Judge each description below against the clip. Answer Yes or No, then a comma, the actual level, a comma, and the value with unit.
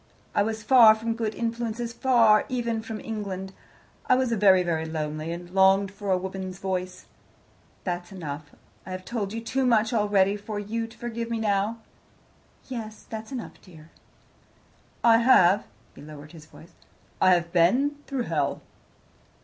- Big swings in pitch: No, average, 3.9 semitones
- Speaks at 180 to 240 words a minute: No, average, 155 wpm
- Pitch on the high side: Yes, high, 205 Hz